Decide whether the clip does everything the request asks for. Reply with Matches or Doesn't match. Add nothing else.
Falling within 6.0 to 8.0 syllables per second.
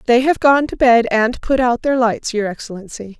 Doesn't match